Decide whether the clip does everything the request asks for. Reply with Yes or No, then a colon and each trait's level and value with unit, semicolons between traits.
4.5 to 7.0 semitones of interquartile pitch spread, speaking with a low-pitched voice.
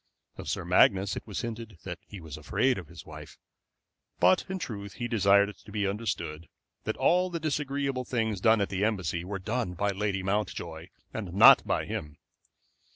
No: average, 3.9 semitones; low, 100 Hz